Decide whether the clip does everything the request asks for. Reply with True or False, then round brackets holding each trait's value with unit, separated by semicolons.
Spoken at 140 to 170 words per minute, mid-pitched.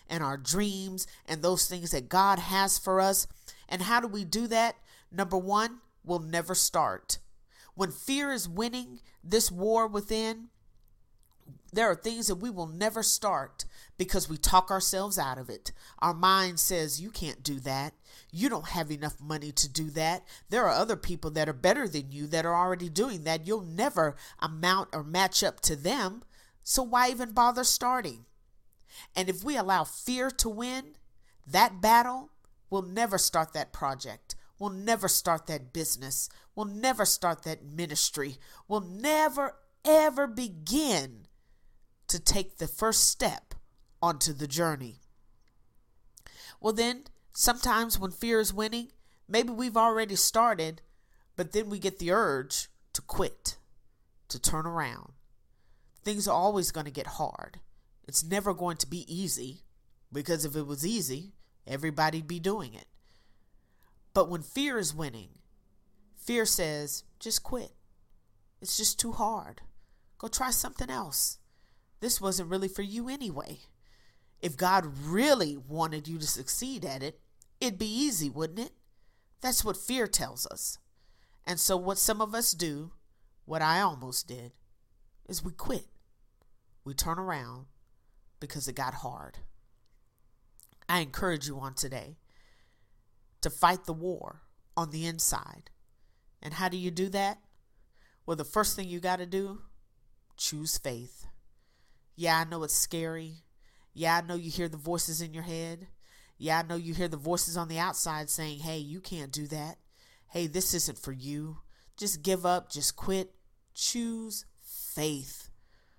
True (155 wpm; 170 Hz)